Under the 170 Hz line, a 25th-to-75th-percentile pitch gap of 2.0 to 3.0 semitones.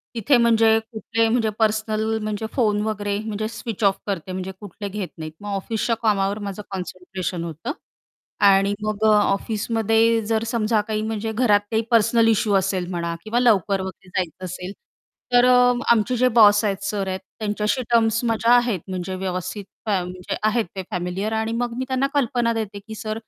No: high, 215 Hz; average, 2.7 semitones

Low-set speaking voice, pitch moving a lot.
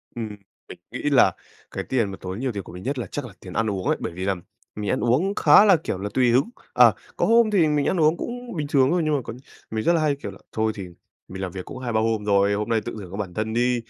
Yes: low, 115 Hz; wide, 6.5 semitones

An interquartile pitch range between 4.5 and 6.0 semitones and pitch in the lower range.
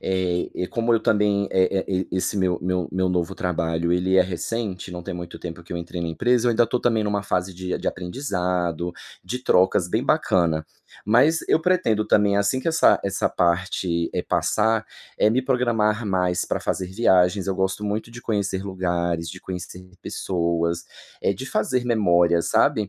No: average, 3.4 semitones; very low, 95 Hz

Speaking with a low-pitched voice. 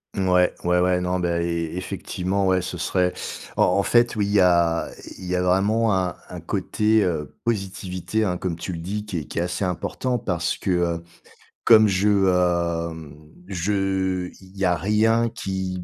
Yes: very low, 90 Hz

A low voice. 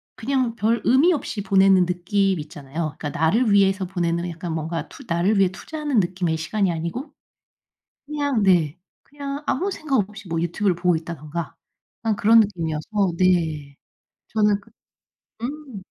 No: high, 190 Hz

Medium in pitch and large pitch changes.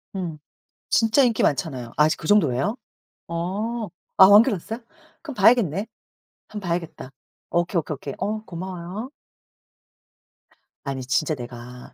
Yes: medium, 175 Hz; wide, 5.8 semitones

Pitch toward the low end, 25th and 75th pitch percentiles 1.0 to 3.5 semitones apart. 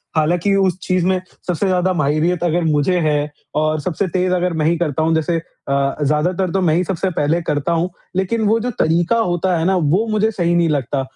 No: medium, 175 Hz; average, 3.1 semitones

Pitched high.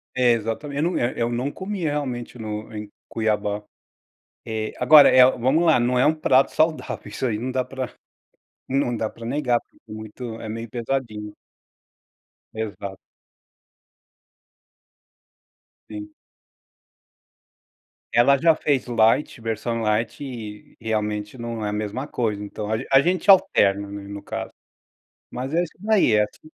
No: low, 120 Hz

